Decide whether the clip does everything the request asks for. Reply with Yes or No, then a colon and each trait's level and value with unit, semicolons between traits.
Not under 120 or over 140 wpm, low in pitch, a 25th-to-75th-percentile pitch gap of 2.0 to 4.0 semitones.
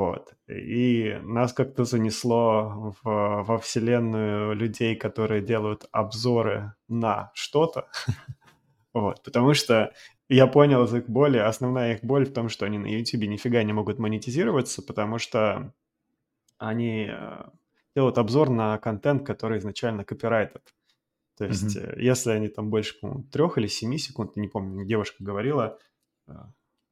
Yes: average, 130 wpm; low, 115 Hz; narrow, 2.5 semitones